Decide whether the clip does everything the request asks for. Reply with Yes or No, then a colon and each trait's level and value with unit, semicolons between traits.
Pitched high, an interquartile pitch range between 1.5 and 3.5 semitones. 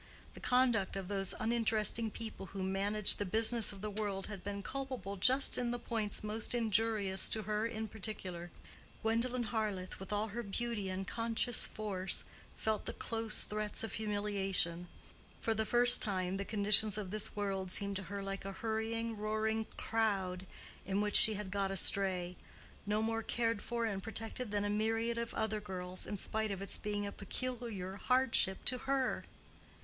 Yes: high, 210 Hz; narrow, 2.4 semitones